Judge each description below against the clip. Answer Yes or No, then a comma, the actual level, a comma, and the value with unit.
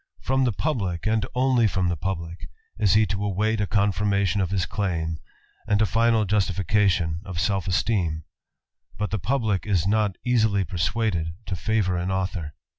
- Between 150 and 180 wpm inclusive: Yes, average, 165 wpm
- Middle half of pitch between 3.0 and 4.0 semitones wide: Yes, average, 3.3 semitones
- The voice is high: No, low, 100 Hz